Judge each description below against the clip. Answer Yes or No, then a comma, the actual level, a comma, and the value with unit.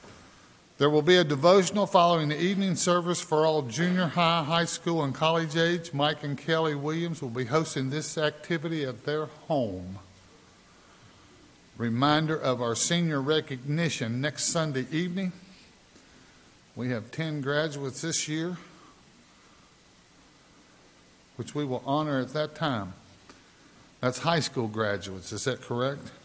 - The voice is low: No, medium, 150 Hz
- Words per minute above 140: No, slow, 135 wpm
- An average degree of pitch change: Yes, average, 4.8 semitones